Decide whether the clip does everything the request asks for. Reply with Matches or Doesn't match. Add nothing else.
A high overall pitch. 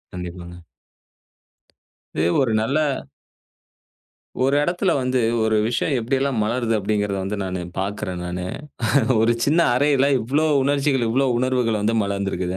Doesn't match